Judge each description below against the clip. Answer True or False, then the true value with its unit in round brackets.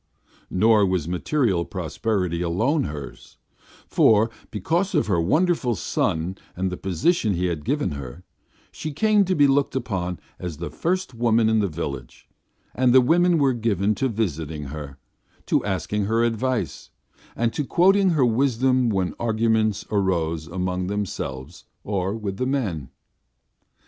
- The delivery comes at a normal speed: True (150 wpm)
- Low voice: True (105 Hz)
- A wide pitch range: True (6.5 semitones)